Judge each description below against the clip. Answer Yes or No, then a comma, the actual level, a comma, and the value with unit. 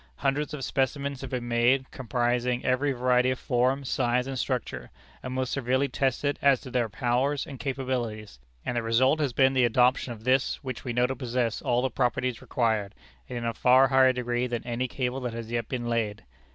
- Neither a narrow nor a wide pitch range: No, narrow, 1.8 semitones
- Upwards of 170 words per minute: Yes, fast, 205 wpm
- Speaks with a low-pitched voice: Yes, low, 125 Hz